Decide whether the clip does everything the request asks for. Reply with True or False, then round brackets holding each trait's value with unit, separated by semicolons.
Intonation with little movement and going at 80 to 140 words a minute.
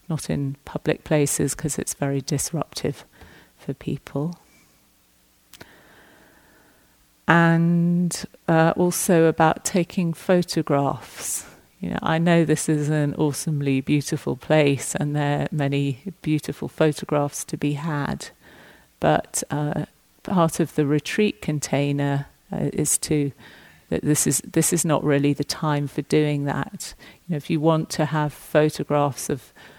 True (2.2 semitones; 135 wpm)